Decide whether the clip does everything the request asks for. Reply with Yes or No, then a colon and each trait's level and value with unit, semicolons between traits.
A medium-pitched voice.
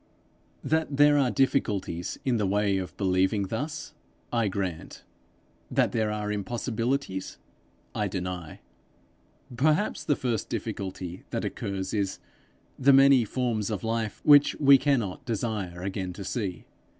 No: low, 105 Hz